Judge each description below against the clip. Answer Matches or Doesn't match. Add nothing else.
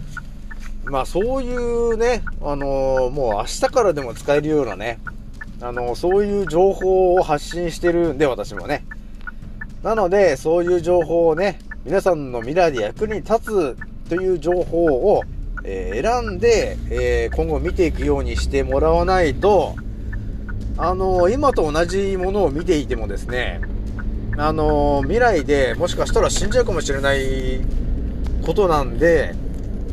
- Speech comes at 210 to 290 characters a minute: Matches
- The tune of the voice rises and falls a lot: Matches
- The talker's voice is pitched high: Doesn't match